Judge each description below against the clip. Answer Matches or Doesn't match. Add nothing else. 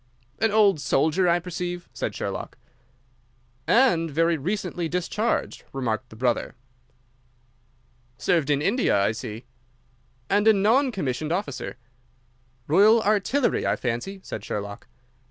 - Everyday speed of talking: Doesn't match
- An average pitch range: Doesn't match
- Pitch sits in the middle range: Matches